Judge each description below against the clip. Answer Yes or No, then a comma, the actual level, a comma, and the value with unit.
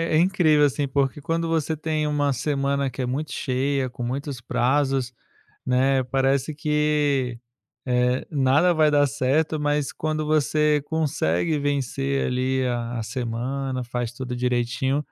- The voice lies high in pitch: No, medium, 140 Hz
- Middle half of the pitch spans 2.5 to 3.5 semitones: Yes, average, 2.9 semitones